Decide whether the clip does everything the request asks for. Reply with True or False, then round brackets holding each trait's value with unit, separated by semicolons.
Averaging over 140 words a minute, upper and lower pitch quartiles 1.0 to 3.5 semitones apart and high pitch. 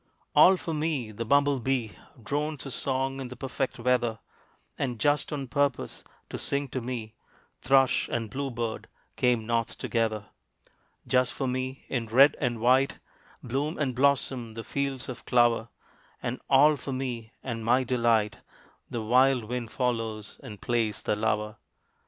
False (155 wpm; 2.9 semitones; 125 Hz)